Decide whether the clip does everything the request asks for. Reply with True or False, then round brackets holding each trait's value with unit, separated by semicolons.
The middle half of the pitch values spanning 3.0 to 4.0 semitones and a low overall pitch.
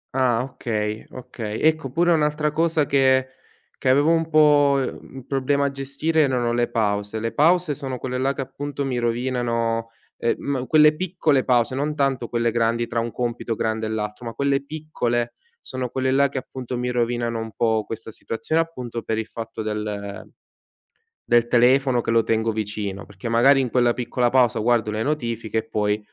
True (3.5 semitones; 125 Hz)